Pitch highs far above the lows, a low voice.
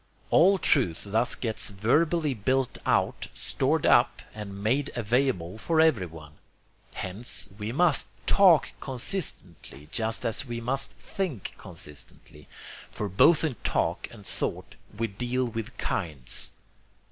Yes: wide, 5.7 semitones; low, 115 Hz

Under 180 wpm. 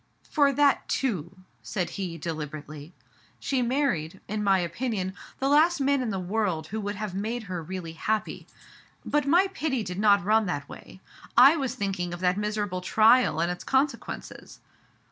Yes: average, 170 wpm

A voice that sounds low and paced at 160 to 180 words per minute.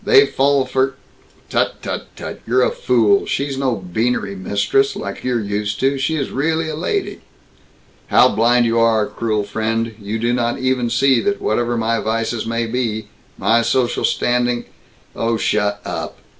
Yes: low, 120 Hz; average, 170 wpm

